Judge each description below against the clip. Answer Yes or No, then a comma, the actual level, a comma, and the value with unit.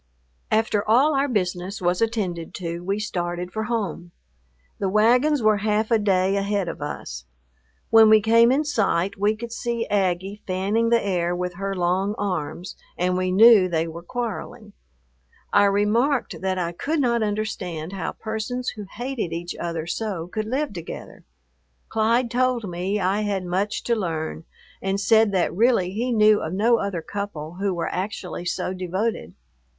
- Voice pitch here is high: Yes, high, 200 Hz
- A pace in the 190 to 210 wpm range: No, average, 165 wpm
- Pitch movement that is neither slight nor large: Yes, average, 3.8 semitones